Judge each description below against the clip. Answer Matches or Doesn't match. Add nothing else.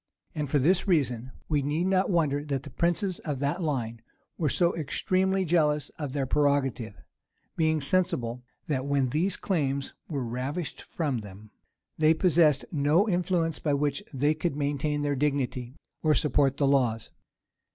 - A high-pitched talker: Doesn't match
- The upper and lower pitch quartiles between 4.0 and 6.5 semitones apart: Doesn't match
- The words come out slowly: Doesn't match